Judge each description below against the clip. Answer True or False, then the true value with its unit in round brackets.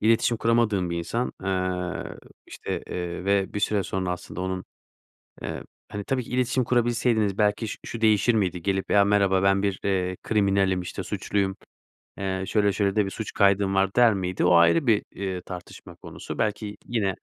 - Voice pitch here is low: True (100 Hz)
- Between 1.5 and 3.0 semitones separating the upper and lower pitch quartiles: True (2.6 semitones)